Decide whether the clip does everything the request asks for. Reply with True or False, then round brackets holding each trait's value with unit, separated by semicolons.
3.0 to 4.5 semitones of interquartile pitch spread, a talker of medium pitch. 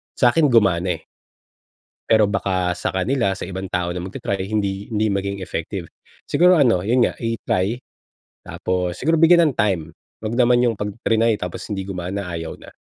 False (4.1 semitones; 100 Hz)